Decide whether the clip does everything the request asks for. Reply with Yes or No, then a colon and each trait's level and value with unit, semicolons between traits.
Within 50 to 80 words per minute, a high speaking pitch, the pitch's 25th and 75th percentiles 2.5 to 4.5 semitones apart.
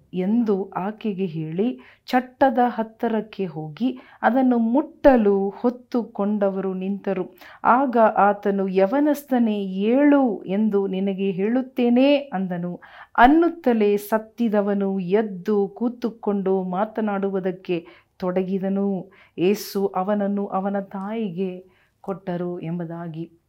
Yes: average, 75 wpm; high, 200 Hz; average, 3.5 semitones